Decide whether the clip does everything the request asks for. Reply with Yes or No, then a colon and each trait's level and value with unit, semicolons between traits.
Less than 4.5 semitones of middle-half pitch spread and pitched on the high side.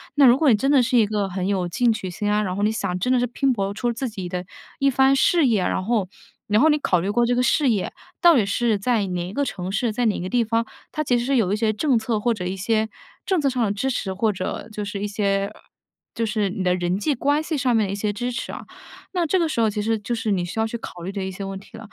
Yes: average, 3.9 semitones; high, 220 Hz